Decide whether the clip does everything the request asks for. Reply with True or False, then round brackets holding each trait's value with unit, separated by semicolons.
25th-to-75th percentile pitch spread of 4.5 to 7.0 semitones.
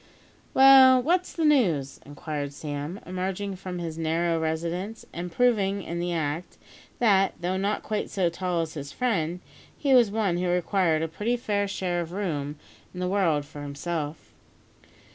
False (4.0 semitones)